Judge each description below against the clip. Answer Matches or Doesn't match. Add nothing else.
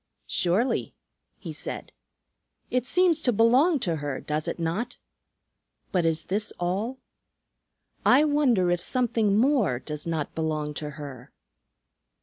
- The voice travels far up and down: Matches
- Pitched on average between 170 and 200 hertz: Matches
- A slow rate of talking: Matches